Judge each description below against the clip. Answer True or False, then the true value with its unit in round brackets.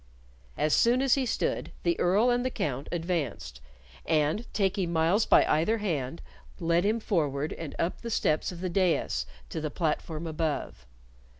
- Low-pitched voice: False (170 Hz)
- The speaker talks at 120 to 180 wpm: True (165 wpm)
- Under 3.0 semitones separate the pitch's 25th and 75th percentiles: False (5.3 semitones)